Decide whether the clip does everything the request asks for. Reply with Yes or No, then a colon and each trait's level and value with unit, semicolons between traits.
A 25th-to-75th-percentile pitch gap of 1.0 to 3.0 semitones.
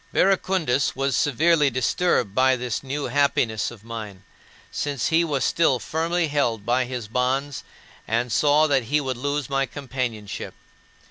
No: average, 3.4 semitones